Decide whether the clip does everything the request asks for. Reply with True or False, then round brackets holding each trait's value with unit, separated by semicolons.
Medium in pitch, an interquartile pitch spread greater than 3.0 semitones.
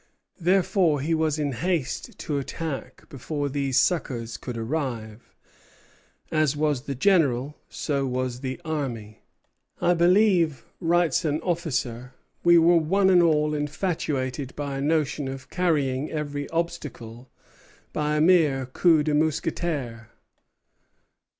True (150 Hz; 4.0 semitones)